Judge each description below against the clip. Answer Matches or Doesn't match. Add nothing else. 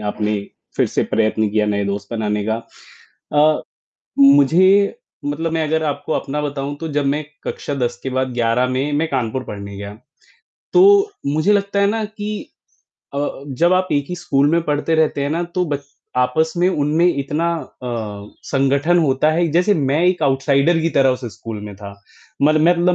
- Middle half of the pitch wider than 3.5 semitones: Matches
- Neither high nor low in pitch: Matches